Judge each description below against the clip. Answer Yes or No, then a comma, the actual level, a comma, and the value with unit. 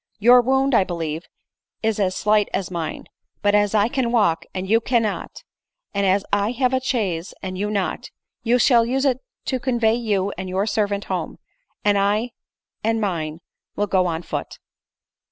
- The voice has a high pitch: Yes, high, 205 Hz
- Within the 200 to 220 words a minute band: No, average, 180 wpm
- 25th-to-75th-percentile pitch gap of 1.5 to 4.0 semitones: Yes, average, 3.7 semitones